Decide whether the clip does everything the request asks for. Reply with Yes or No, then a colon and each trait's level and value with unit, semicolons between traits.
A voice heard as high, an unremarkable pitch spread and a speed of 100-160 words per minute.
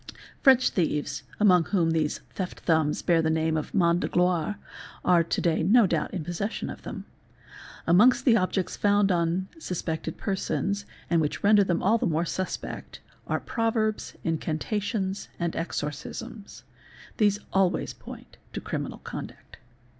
No: medium, 180 Hz; average, 3.8 semitones; average, 150 wpm